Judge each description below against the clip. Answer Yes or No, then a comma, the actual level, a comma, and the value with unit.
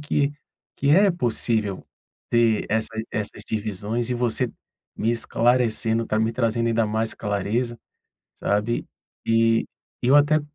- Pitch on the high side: No, low, 115 Hz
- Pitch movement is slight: Yes, narrow, 1.8 semitones